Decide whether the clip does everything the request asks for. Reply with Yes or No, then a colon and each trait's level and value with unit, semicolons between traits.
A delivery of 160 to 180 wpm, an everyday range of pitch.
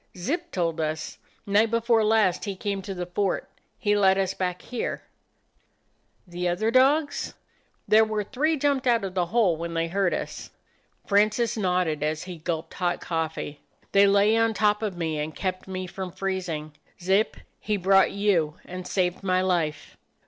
Yes: average, 170 wpm; average, 3.4 semitones